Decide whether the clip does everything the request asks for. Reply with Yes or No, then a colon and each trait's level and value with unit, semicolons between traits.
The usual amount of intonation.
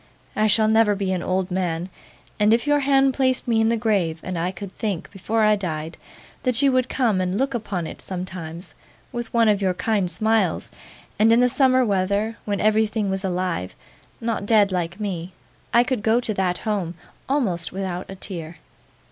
Yes: average, 3.7 semitones